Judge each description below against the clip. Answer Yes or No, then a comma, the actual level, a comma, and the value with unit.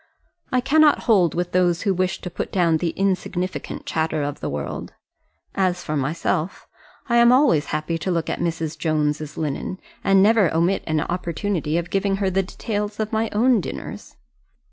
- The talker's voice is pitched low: No, medium, 180 Hz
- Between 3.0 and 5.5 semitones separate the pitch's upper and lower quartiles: Yes, average, 4.0 semitones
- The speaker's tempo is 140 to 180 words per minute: Yes, average, 175 wpm